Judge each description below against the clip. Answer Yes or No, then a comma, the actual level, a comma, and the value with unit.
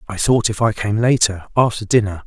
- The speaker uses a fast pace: Yes, fast, 210 wpm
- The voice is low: Yes, low, 105 Hz